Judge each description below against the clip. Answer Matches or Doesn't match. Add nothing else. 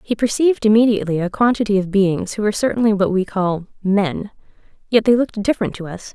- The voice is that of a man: Doesn't match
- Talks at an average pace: Matches